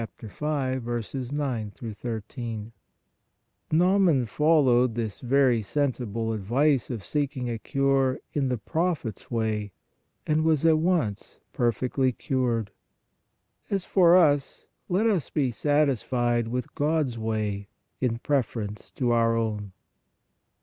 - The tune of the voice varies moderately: Yes, average, 4.5 semitones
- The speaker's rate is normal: No, slow, 120 wpm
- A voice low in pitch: Yes, low, 125 Hz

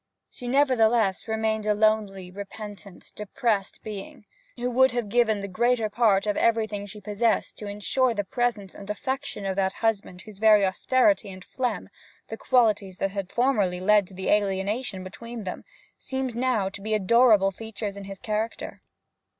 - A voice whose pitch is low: No, high, 210 Hz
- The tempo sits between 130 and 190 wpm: Yes, average, 160 wpm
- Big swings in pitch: No, average, 2.9 semitones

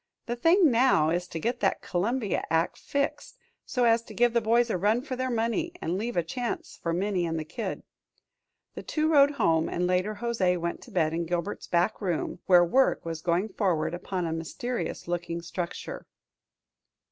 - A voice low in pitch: No, high, 195 Hz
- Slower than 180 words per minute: No, average, 185 wpm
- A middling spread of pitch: No, wide, 6.0 semitones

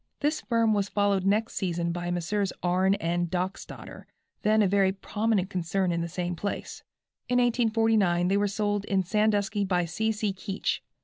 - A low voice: No, high, 195 Hz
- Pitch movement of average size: Yes, average, 3.0 semitones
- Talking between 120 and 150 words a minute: No, average, 175 wpm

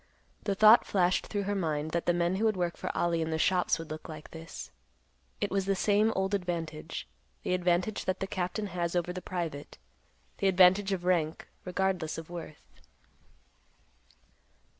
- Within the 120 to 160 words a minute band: No, average, 175 wpm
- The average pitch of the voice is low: No, medium, 180 Hz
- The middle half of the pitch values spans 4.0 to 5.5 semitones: No, narrow, 2.6 semitones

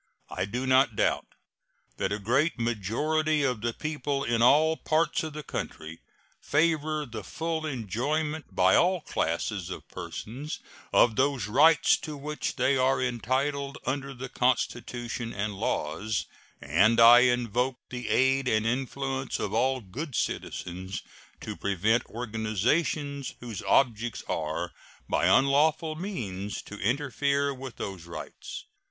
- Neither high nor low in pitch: No, low, 130 Hz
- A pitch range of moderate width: Yes, average, 4.8 semitones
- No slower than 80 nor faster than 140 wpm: Yes, slow, 135 wpm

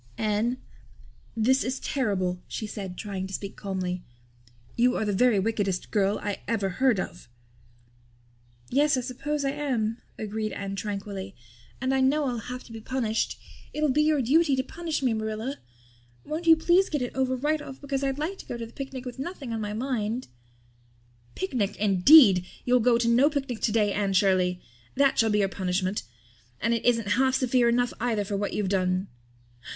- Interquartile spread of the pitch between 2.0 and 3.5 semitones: No, average, 4.7 semitones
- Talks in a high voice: Yes, high, 230 Hz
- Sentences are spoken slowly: No, average, 185 wpm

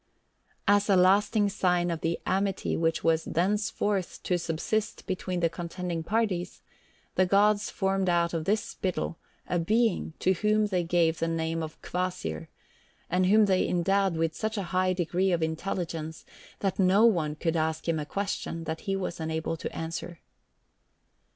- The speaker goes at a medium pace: Yes, average, 165 wpm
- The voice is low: No, medium, 180 Hz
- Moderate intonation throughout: Yes, average, 3.1 semitones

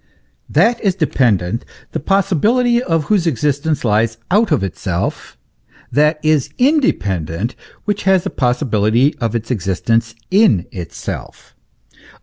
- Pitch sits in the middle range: Yes, medium, 145 Hz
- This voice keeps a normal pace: No, slow, 120 wpm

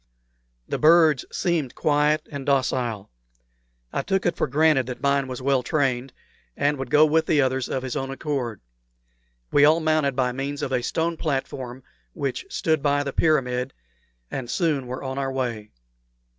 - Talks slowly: No, average, 170 wpm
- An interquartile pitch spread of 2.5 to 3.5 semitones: Yes, average, 2.8 semitones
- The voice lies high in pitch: No, medium, 140 Hz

